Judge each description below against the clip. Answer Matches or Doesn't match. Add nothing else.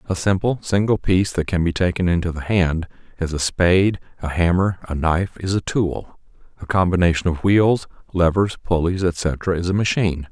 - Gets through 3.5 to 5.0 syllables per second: Doesn't match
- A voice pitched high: Doesn't match